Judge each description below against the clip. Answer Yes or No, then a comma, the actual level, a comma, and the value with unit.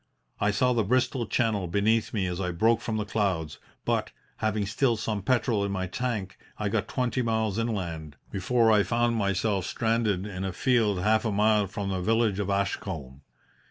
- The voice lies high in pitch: No, low, 105 Hz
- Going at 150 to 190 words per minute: Yes, average, 185 wpm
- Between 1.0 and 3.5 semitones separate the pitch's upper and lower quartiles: Yes, average, 2.9 semitones